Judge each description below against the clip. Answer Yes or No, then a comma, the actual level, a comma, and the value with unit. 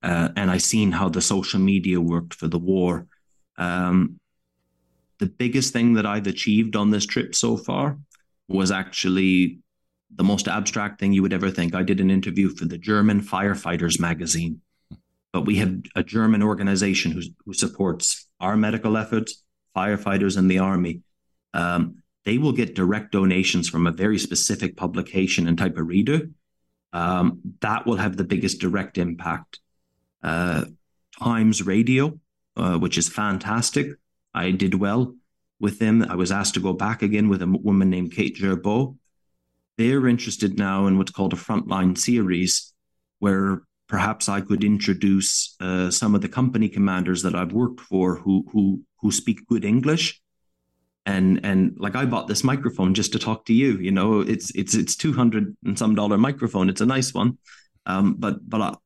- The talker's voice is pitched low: Yes, very low, 95 Hz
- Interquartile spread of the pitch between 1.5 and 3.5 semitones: Yes, average, 3.2 semitones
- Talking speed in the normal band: Yes, average, 170 wpm